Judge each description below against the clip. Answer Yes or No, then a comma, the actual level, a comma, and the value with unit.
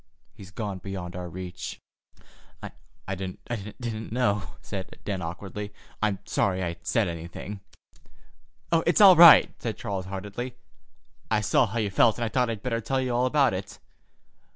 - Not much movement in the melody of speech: No, average, 4.0 semitones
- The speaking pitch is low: Yes, low, 105 Hz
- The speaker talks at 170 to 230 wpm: No, average, 155 wpm